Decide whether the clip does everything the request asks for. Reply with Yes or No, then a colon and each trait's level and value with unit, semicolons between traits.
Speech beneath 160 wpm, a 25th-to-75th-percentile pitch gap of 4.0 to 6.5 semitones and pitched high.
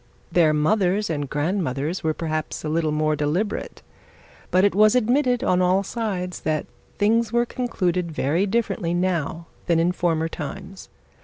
No: average, 150 wpm; average, 4.6 semitones; medium, 180 Hz